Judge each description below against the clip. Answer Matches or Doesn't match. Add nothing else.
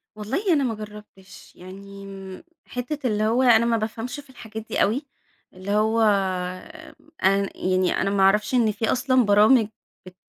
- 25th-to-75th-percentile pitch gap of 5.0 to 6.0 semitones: Doesn't match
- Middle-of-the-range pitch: Doesn't match